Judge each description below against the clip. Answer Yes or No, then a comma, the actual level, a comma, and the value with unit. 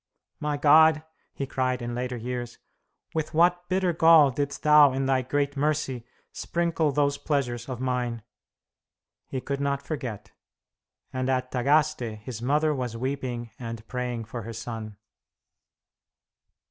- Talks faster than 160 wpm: No, slow, 135 wpm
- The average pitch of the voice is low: Yes, low, 130 Hz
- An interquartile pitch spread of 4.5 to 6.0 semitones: No, average, 3.5 semitones